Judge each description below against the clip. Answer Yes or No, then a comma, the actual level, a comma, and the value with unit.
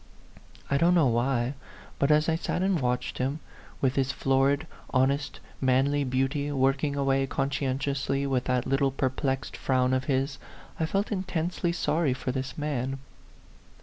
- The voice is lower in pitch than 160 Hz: Yes, low, 135 Hz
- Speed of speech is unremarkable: Yes, average, 150 wpm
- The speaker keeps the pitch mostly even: Yes, narrow, 1.9 semitones